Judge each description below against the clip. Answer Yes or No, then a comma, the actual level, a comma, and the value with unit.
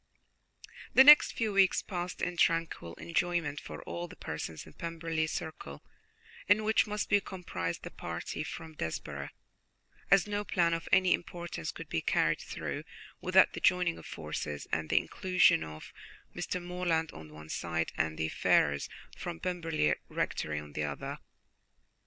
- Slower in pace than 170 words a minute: Yes, average, 160 wpm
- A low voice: No, medium, 165 Hz